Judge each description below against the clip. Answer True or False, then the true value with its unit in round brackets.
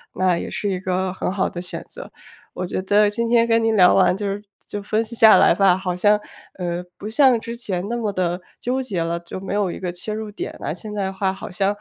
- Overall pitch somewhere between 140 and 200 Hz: True (195 Hz)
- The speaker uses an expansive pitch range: False (3.1 semitones)